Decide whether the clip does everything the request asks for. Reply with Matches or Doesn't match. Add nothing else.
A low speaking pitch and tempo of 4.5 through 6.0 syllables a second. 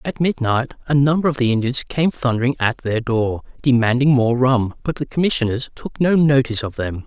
Matches